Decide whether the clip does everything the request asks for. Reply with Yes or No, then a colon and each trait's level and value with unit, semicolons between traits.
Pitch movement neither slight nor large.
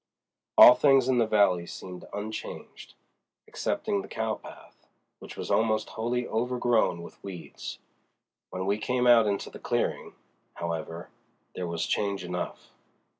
Yes: average, 5.0 semitones